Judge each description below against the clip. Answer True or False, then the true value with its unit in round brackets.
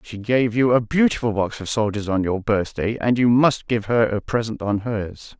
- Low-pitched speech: True (110 Hz)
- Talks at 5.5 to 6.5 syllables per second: False (4.8 syllables/s)